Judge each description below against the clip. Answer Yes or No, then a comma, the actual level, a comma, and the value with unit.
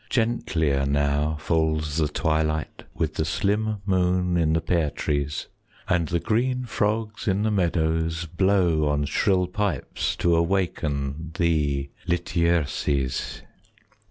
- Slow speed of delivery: Yes, slow, 125 wpm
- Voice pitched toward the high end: No, very low, 80 Hz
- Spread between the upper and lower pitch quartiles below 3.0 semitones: No, average, 3.6 semitones